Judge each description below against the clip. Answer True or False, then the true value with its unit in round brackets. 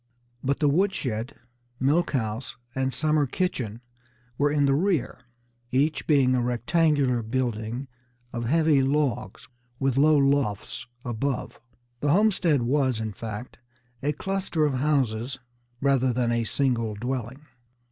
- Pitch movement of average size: True (3.6 semitones)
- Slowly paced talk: True (130 wpm)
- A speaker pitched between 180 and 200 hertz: False (135 Hz)